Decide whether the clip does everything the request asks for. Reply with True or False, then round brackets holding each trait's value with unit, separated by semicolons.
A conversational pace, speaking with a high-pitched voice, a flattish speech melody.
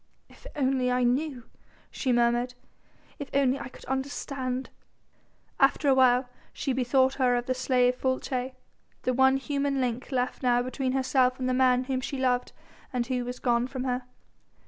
True (170 wpm; 255 Hz; 1.2 semitones)